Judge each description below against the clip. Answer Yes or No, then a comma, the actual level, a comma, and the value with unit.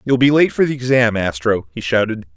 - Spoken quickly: Yes, fast, 230 wpm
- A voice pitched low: Yes, low, 110 Hz